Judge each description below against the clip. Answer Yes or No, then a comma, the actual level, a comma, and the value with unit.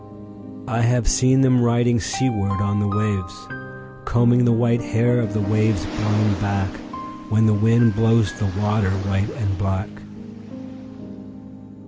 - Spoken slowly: Yes, slow, 125 wpm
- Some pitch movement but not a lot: Yes, average, 3.0 semitones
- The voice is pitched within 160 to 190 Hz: No, low, 105 Hz